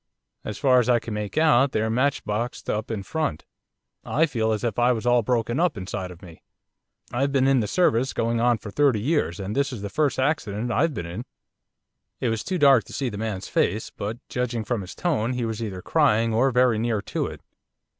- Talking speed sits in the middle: No, fast, 220 wpm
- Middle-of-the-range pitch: No, low, 115 Hz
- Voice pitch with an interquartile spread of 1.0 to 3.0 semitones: No, average, 3.8 semitones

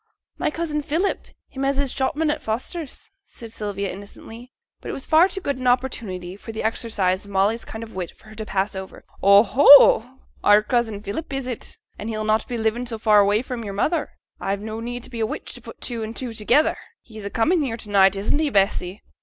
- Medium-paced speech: No, fast, 225 wpm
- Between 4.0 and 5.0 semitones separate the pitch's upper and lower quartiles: Yes, average, 4.4 semitones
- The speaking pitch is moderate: No, high, 225 Hz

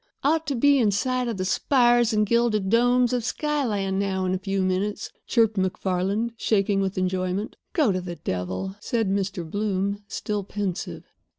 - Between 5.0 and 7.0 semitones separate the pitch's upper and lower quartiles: No, average, 3.8 semitones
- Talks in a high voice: Yes, high, 205 Hz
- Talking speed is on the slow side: No, average, 170 wpm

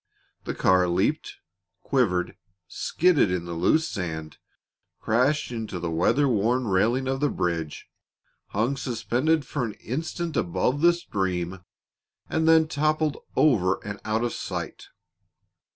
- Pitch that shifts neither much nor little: No, wide, 8.1 semitones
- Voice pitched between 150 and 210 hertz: No, low, 115 Hz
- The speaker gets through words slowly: Yes, slow, 130 wpm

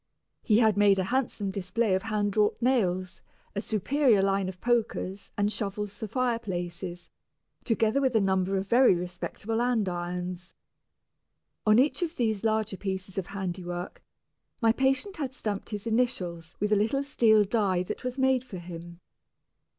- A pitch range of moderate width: Yes, average, 4.0 semitones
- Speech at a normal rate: Yes, average, 155 wpm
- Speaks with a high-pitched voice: Yes, high, 205 Hz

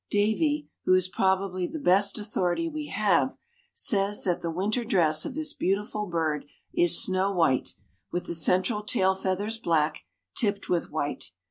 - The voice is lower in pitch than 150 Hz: No, high, 190 Hz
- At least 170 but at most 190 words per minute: No, average, 155 wpm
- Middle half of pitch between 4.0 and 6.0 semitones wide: No, average, 3.2 semitones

